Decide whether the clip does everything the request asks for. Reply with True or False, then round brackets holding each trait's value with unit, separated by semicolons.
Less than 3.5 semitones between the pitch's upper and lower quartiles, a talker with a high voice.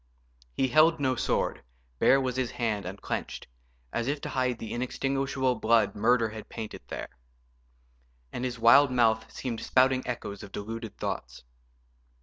False (2.8 semitones; 120 Hz)